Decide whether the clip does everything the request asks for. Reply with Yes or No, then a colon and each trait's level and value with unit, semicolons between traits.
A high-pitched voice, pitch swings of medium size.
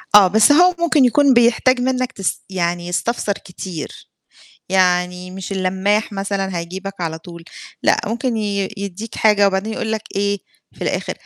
Yes: high, 200 Hz; average, 3.5 semitones